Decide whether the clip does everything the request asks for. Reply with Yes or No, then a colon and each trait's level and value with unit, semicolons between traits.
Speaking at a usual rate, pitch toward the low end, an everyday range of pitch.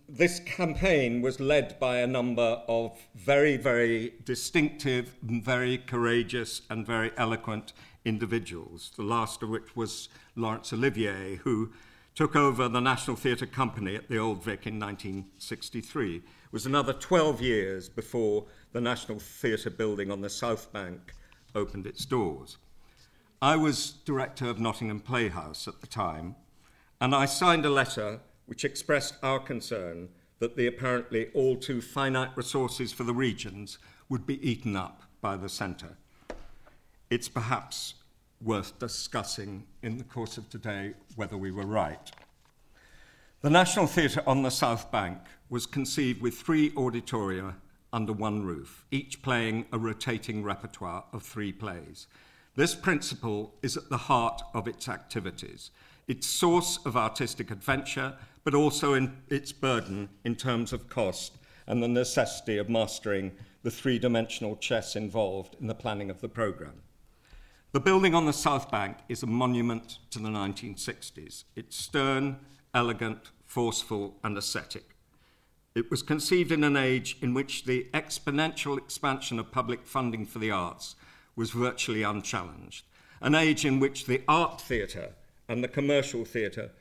Yes: average, 145 wpm; low, 120 Hz; average, 3.6 semitones